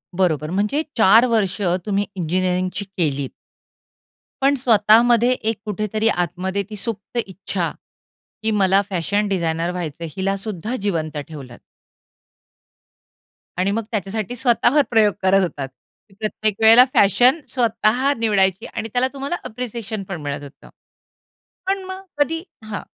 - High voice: Yes, high, 205 Hz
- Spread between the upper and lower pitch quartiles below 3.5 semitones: No, average, 3.8 semitones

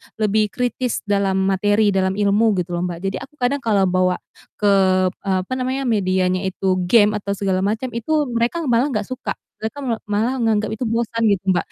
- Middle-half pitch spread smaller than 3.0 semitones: No, average, 3.4 semitones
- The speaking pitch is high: Yes, high, 210 Hz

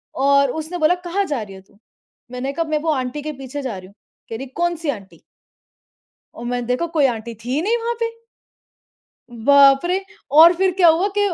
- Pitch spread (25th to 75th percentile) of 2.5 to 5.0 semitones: No, wide, 5.5 semitones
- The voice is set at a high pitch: Yes, very high, 280 Hz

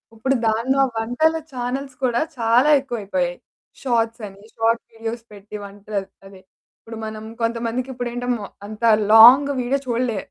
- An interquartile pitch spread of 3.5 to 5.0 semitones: No, narrow, 2.4 semitones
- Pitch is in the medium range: No, high, 230 Hz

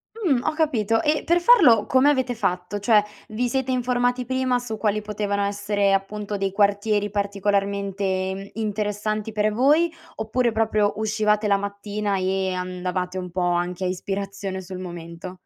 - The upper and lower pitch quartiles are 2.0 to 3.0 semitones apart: Yes, average, 2.7 semitones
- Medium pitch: No, high, 205 Hz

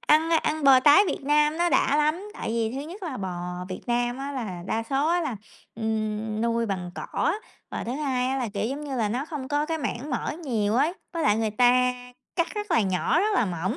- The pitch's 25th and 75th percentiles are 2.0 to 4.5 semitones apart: No, average, 5.3 semitones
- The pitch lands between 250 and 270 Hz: Yes, very high, 255 Hz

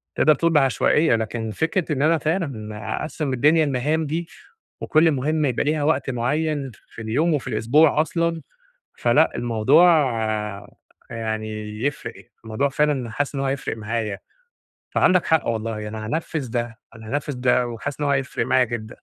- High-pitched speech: No, low, 135 Hz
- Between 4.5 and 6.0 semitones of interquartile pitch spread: Yes, average, 5.1 semitones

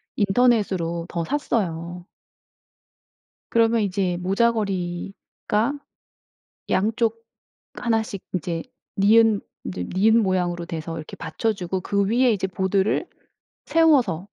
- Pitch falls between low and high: No, high, 200 Hz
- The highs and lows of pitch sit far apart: No, average, 4.4 semitones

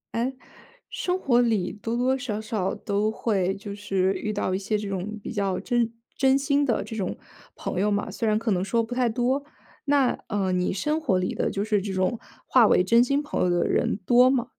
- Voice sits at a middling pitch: No, high, 220 Hz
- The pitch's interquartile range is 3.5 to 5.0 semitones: Yes, average, 4.1 semitones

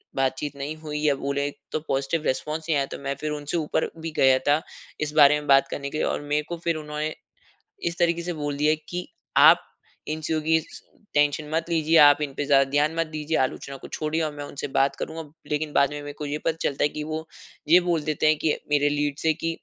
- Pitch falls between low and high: Yes, medium, 150 Hz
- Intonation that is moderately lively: No, narrow, 1.7 semitones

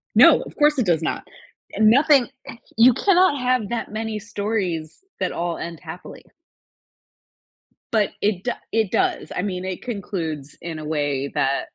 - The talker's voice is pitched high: Yes, high, 200 Hz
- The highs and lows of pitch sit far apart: Yes, wide, 6.0 semitones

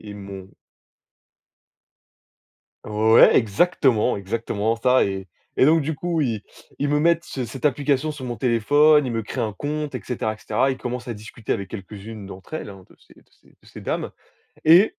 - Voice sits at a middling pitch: No, low, 120 Hz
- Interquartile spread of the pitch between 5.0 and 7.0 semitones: Yes, wide, 5.5 semitones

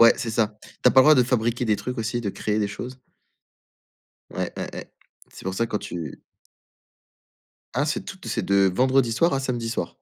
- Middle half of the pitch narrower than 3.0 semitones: No, average, 3.4 semitones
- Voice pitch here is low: Yes, low, 115 Hz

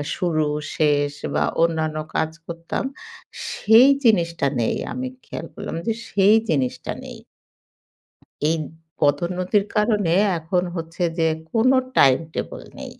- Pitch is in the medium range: Yes, medium, 165 Hz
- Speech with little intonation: No, average, 4.8 semitones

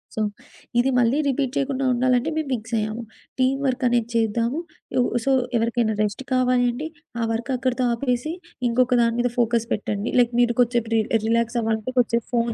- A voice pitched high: Yes, high, 240 Hz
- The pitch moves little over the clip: Yes, narrow, 1.7 semitones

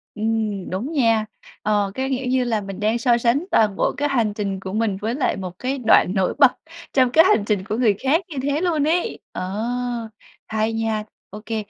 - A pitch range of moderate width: Yes, average, 4.2 semitones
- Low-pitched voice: No, high, 225 Hz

